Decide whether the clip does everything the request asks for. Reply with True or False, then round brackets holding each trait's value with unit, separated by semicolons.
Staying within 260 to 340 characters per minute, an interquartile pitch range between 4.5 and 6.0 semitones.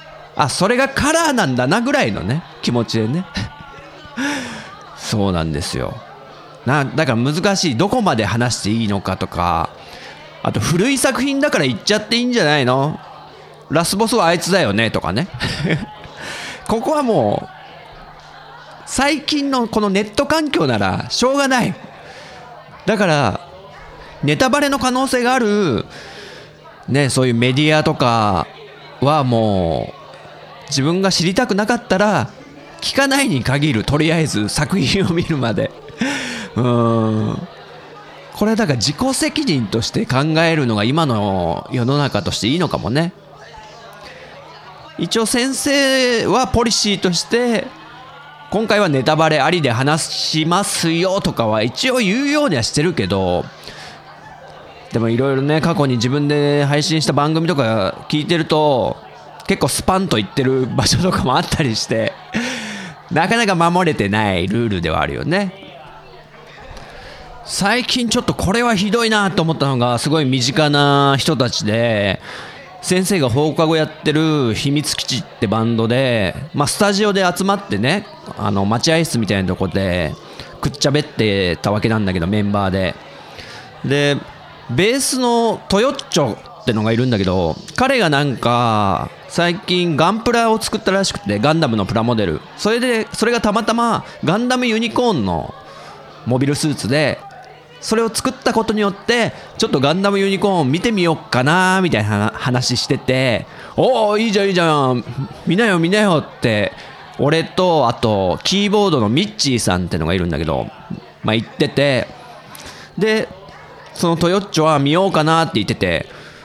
False (305 characters per minute; 9.0 semitones)